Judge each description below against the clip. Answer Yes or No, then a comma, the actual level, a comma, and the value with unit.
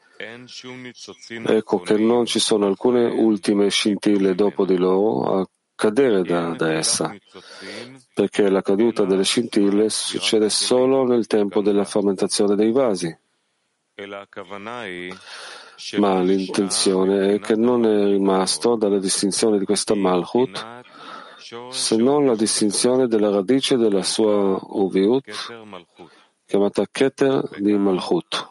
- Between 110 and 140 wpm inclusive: Yes, slow, 115 wpm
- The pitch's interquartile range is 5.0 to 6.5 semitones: No, average, 3.2 semitones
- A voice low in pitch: Yes, low, 105 Hz